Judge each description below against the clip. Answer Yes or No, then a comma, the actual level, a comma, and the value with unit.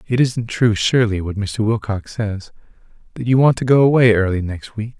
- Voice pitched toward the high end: No, low, 110 Hz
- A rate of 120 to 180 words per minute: No, fast, 205 wpm